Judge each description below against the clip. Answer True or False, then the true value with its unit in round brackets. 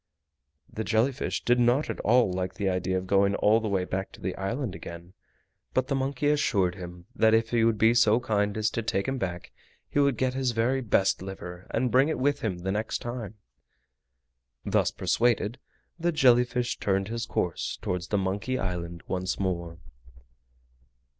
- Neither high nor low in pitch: False (110 Hz)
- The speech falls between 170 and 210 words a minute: True (185 wpm)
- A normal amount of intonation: True (4.6 semitones)